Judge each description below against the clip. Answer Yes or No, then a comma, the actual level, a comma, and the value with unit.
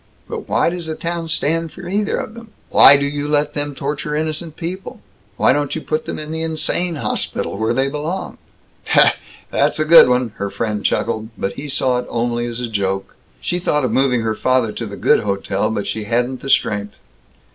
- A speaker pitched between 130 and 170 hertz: Yes, medium, 140 Hz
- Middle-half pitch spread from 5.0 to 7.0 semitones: Yes, wide, 5.6 semitones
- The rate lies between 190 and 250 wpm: Yes, average, 200 wpm